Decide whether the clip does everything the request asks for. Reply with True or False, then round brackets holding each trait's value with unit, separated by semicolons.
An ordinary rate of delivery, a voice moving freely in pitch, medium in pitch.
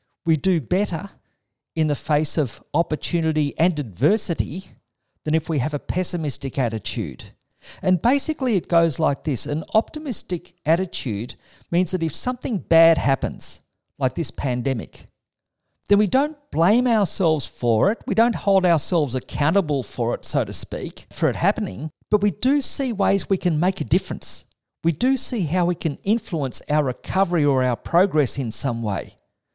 True (160 wpm; 6.1 semitones; 165 Hz)